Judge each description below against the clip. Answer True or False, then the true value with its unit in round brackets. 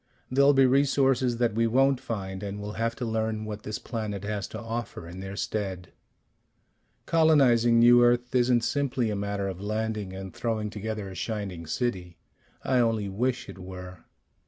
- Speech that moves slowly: False (170 wpm)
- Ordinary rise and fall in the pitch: True (3.5 semitones)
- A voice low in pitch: True (110 Hz)